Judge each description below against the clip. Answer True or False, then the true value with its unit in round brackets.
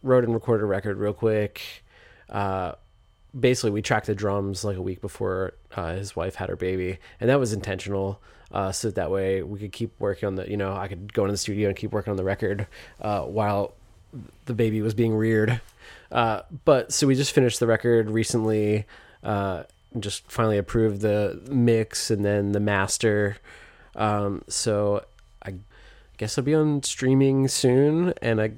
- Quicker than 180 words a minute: True (190 wpm)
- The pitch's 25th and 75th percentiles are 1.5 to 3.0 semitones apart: True (2.6 semitones)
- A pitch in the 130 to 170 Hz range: False (105 Hz)